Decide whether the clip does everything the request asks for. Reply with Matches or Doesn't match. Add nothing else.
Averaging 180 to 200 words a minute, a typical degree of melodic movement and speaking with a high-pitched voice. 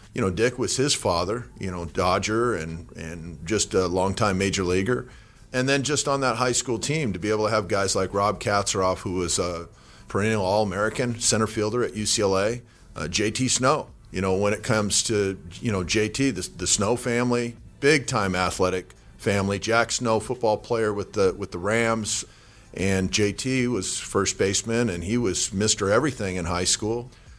Doesn't match